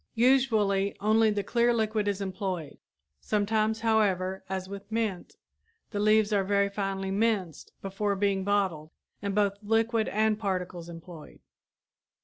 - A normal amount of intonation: No, narrow, 2.2 semitones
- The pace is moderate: No, slow, 130 wpm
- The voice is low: No, high, 205 Hz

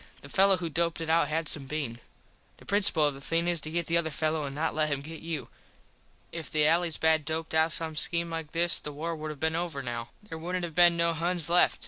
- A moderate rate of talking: No, fast, 255 wpm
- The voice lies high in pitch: No, medium, 160 Hz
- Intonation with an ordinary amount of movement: No, narrow, 1.7 semitones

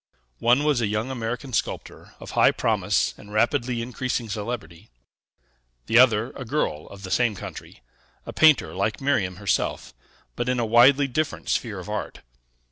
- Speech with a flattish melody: No, average, 3.5 semitones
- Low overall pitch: Yes, low, 120 Hz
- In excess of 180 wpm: No, average, 160 wpm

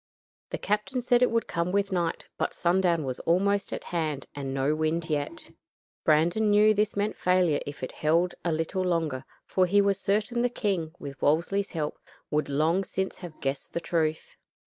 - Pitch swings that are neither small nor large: Yes, average, 4.4 semitones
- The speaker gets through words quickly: No, average, 185 wpm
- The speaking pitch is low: No, medium, 175 Hz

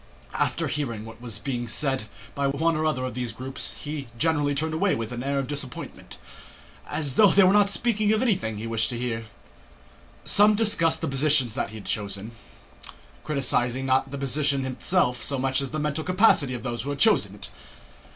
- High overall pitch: No, medium, 140 Hz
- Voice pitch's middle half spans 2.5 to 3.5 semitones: No, average, 4.5 semitones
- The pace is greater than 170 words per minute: Yes, average, 195 wpm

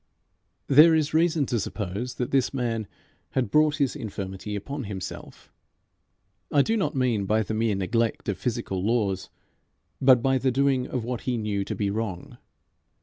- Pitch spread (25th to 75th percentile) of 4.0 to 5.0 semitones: Yes, average, 4.7 semitones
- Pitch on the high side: No, low, 120 Hz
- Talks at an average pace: Yes, average, 165 wpm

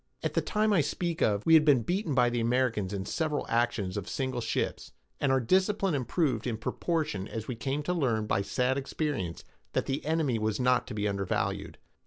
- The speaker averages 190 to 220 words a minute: Yes, fast, 205 wpm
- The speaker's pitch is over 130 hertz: No, low, 125 Hz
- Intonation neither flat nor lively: No, wide, 6.0 semitones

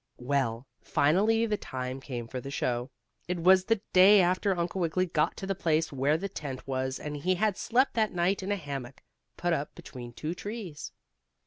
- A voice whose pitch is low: No, medium, 170 Hz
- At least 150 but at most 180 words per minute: No, average, 195 wpm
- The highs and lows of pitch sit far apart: Yes, wide, 6.1 semitones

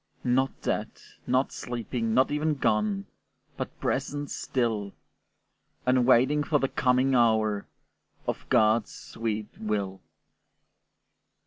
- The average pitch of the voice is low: Yes, low, 120 Hz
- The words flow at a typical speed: No, slow, 105 wpm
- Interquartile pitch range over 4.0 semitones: No, average, 3.6 semitones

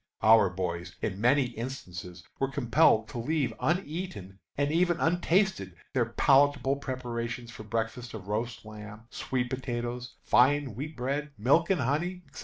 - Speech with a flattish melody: No, average, 4.5 semitones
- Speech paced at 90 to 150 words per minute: Yes, average, 145 wpm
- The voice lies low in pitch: Yes, low, 125 Hz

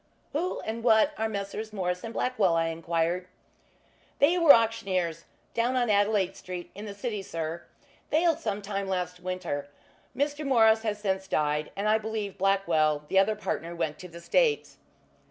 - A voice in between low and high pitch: No, high, 200 Hz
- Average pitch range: Yes, average, 4.0 semitones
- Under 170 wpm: Yes, average, 160 wpm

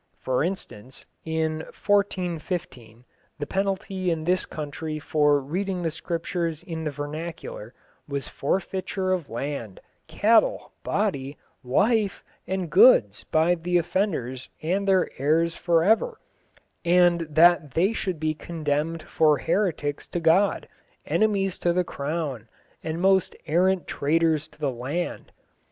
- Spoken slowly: Yes, slow, 125 wpm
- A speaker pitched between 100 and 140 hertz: No, medium, 165 Hz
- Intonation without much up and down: No, average, 3.9 semitones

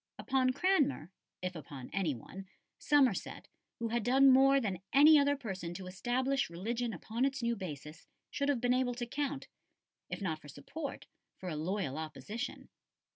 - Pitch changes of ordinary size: No, wide, 6.8 semitones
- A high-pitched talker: Yes, high, 235 Hz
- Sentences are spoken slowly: No, average, 165 wpm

